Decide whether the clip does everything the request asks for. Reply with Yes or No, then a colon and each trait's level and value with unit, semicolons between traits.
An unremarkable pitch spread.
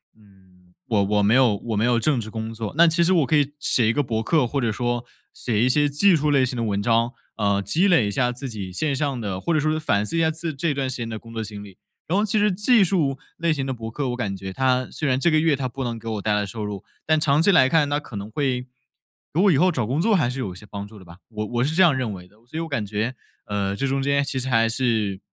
No: wide, 5.7 semitones